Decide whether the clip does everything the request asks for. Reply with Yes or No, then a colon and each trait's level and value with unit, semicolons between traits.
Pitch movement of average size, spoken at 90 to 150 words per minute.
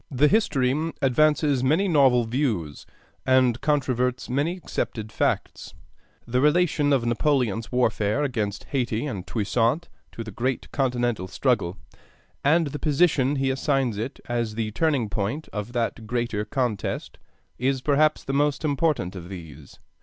Yes: average, 4.3 semitones; average, 140 wpm